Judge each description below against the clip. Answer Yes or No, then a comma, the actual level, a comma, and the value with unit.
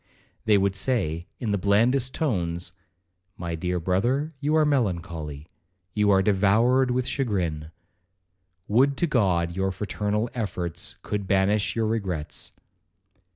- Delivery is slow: Yes, slow, 115 wpm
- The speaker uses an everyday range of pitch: Yes, average, 4.7 semitones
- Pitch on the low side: Yes, low, 100 Hz